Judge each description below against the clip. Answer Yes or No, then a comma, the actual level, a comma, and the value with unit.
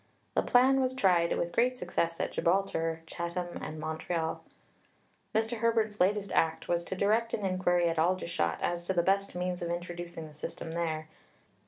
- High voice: No, medium, 175 Hz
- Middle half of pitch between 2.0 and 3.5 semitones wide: Yes, average, 3.1 semitones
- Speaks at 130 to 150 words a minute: No, average, 170 wpm